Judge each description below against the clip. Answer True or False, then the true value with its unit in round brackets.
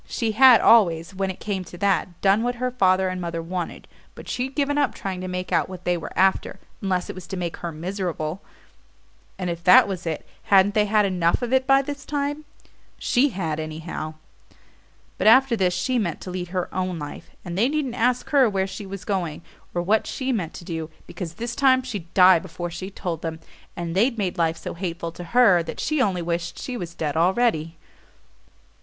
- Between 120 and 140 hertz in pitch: False (185 Hz)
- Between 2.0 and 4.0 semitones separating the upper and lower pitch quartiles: False (5.2 semitones)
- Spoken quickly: True (210 wpm)